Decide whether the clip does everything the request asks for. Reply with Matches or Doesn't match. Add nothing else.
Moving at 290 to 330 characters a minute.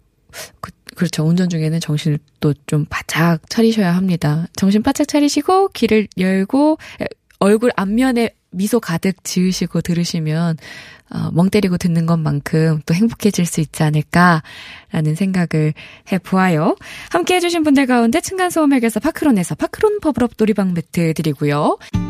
Matches